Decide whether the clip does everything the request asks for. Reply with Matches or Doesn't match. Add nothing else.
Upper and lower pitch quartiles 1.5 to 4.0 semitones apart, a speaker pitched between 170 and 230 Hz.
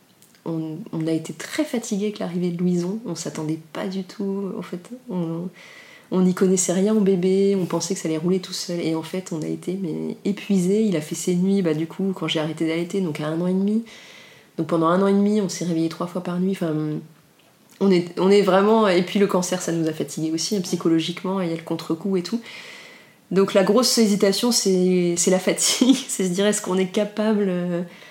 Matches